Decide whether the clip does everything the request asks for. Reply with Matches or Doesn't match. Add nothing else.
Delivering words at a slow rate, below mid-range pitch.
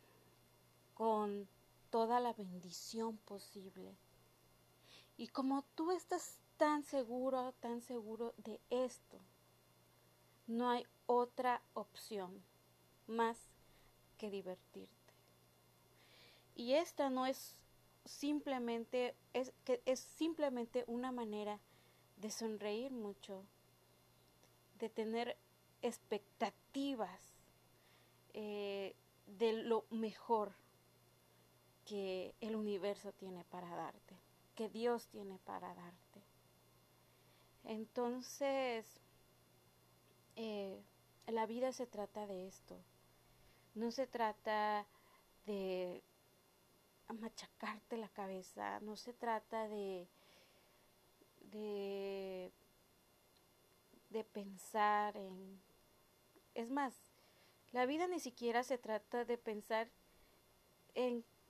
Doesn't match